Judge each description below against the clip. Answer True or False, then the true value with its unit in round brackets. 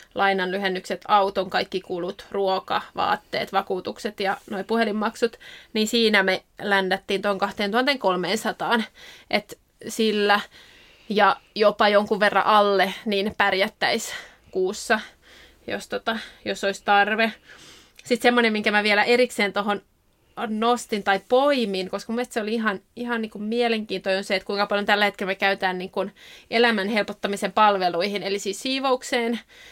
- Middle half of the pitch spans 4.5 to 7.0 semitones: False (2.6 semitones)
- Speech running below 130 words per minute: False (135 wpm)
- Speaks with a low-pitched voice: False (205 Hz)